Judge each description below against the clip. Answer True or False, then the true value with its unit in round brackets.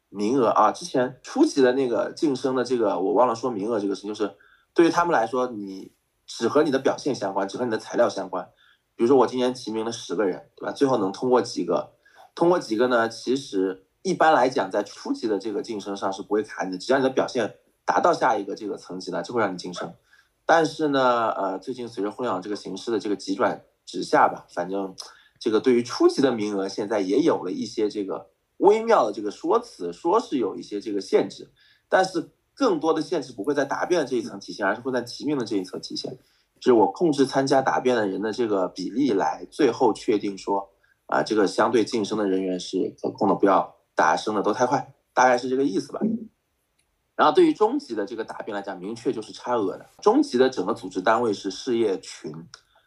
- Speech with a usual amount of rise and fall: False (5.9 semitones)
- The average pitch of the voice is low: True (125 Hz)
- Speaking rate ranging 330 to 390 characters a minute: True (335 characters per minute)